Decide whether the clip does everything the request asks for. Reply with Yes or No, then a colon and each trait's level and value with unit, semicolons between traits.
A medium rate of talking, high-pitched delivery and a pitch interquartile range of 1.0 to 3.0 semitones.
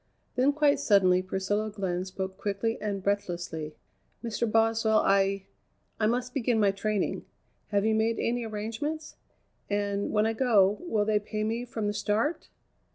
Yes: average, 155 wpm; high, 215 Hz; narrow, 2.4 semitones